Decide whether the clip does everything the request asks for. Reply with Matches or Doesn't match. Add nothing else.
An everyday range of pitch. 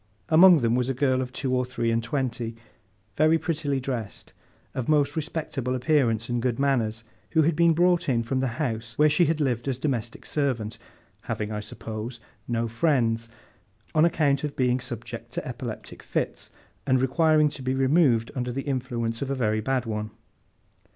Matches